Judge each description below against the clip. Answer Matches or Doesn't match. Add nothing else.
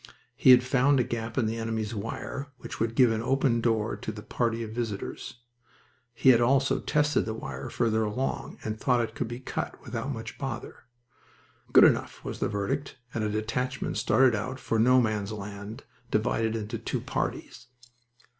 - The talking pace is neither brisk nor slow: Matches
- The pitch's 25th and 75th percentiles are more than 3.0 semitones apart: Doesn't match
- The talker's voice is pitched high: Doesn't match